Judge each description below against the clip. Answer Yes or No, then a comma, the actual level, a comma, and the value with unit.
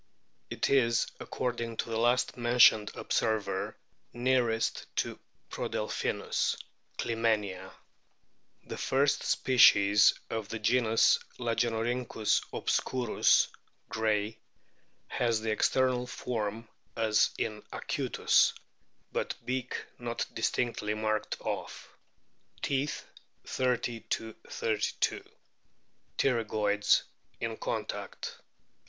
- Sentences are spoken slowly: Yes, slow, 85 wpm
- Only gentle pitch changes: Yes, narrow, 2.2 semitones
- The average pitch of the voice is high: No, low, 115 Hz